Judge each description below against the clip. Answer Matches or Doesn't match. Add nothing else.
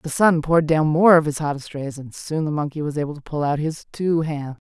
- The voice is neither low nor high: Matches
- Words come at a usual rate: Doesn't match